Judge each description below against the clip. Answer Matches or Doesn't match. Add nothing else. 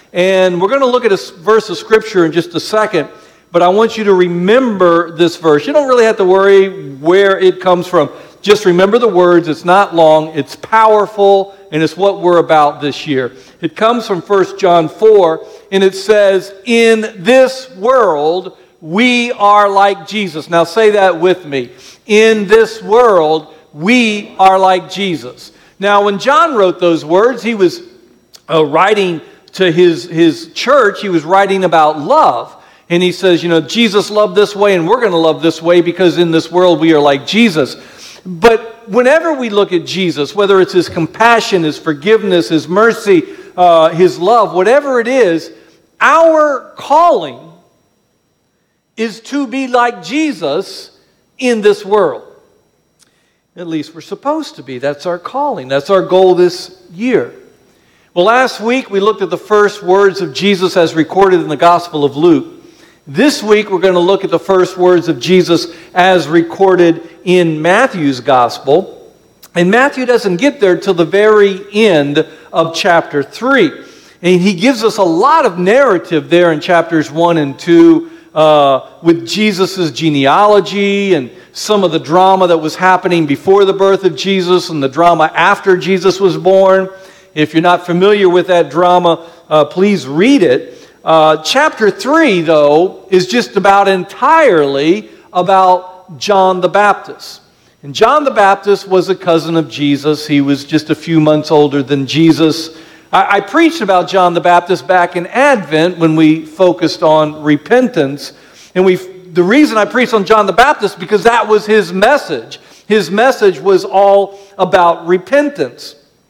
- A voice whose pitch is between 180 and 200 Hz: Matches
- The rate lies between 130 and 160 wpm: Doesn't match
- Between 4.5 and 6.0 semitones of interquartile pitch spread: Doesn't match